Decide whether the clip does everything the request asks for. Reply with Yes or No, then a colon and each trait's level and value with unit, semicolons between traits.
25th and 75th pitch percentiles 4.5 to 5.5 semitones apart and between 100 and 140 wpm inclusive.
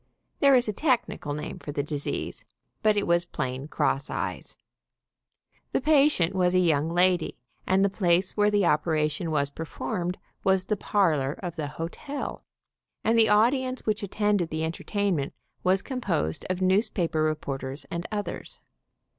No: average, 5.0 semitones; average, 155 wpm